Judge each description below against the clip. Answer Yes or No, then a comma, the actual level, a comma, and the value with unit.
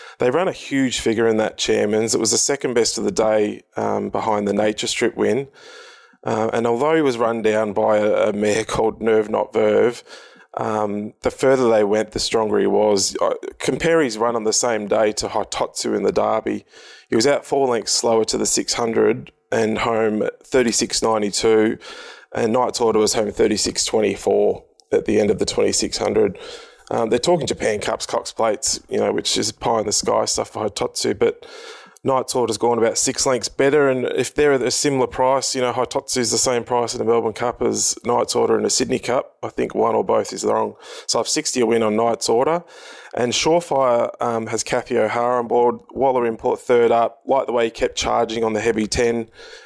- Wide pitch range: Yes, wide, 6.6 semitones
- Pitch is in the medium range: No, low, 120 Hz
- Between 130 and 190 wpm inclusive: No, fast, 205 wpm